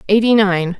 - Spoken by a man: No, female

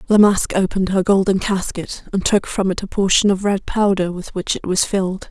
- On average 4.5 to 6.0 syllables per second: Yes, 5.4 syllables/s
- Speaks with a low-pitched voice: No, high, 190 Hz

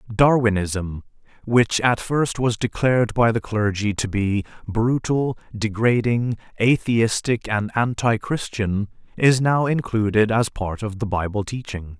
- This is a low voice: Yes, low, 110 Hz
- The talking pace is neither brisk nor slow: No, slow, 130 wpm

